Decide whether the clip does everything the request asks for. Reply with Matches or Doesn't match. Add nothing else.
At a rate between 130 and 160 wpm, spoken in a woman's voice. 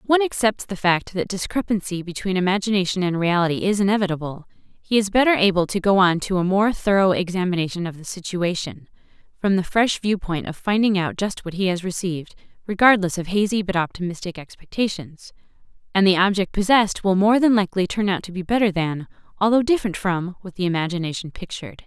Doesn't match